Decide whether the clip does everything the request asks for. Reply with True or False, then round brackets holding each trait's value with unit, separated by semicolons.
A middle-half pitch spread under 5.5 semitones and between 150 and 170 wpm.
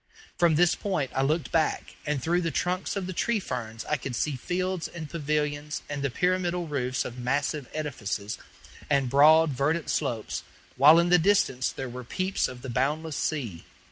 False (4.6 semitones; 180 wpm)